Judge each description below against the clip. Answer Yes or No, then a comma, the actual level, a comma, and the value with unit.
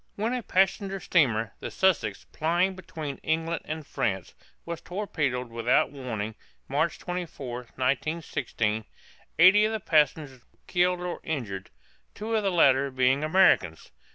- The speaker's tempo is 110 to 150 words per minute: Yes, slow, 135 wpm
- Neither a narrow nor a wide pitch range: No, wide, 6.2 semitones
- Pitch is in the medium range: Yes, medium, 155 Hz